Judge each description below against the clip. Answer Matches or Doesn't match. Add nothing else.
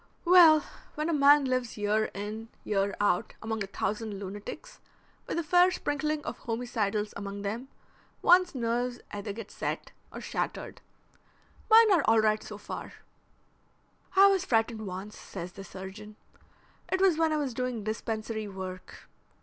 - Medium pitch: Doesn't match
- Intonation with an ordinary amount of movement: Doesn't match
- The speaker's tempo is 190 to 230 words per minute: Doesn't match